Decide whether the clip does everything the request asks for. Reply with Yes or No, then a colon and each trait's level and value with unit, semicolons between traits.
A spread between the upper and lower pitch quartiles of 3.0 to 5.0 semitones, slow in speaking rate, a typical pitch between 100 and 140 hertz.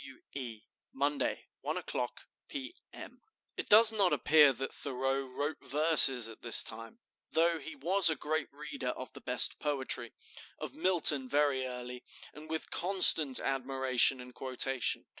No: average, 3.5 semitones; average, 150 wpm; low, 135 Hz